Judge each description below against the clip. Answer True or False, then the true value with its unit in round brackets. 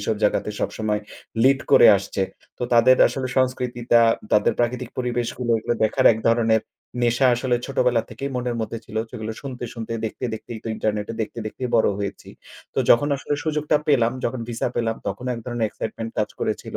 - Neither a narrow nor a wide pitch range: False (2.2 semitones)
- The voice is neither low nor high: False (120 Hz)